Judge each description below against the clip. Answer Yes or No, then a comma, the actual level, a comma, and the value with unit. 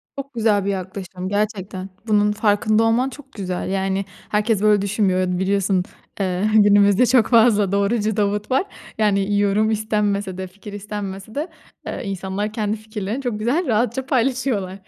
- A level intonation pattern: Yes, narrow, 2.1 semitones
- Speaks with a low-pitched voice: No, high, 205 Hz